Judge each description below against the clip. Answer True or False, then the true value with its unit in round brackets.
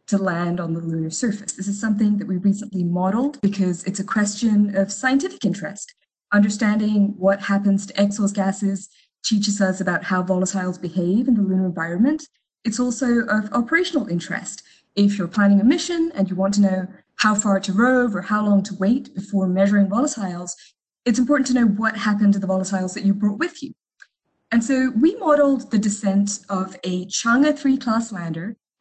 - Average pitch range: True (3.5 semitones)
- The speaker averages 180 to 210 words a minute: True (185 wpm)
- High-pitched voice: True (205 Hz)